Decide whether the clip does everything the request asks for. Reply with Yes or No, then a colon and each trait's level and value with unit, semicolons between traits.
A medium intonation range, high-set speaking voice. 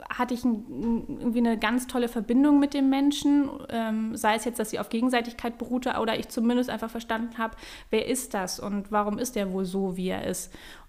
No: narrow, 2.2 semitones; high, 235 Hz